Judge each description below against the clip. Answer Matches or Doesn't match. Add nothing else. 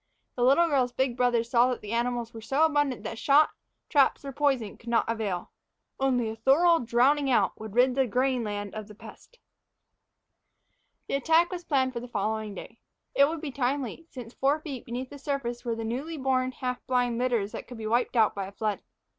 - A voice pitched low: Doesn't match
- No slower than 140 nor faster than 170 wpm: Doesn't match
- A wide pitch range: Doesn't match